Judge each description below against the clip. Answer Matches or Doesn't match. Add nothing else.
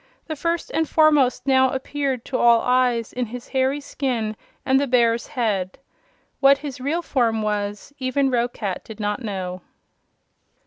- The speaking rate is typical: Matches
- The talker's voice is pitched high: Matches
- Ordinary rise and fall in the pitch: Matches